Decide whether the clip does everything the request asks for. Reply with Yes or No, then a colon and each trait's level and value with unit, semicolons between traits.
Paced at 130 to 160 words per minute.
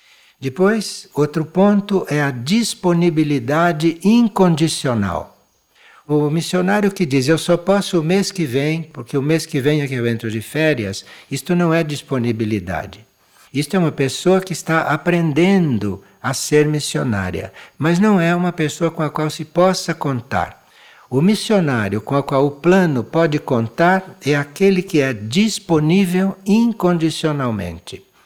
Yes: average, 145 wpm